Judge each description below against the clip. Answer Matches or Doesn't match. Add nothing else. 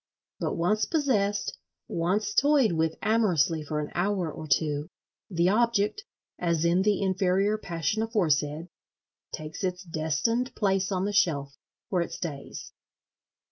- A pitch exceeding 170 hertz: Matches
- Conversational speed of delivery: Doesn't match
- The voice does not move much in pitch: Doesn't match